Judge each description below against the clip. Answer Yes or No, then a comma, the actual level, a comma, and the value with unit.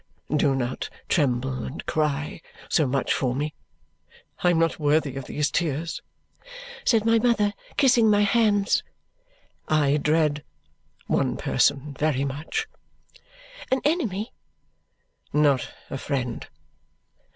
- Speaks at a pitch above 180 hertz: No, medium, 150 Hz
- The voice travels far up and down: Yes, wide, 6.7 semitones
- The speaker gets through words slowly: Yes, slow, 115 wpm